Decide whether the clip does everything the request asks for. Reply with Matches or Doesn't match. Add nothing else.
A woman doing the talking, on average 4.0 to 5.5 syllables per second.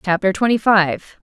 Matches